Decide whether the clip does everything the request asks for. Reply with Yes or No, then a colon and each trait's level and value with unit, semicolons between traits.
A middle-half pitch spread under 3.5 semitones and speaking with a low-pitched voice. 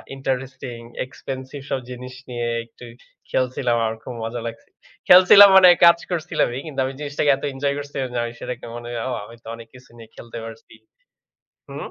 Yes: average, 3.0 semitones; low, 130 Hz